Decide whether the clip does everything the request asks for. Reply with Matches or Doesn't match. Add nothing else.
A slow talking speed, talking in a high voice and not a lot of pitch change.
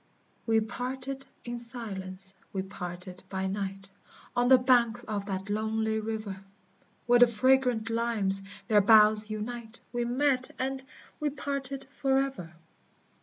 Doesn't match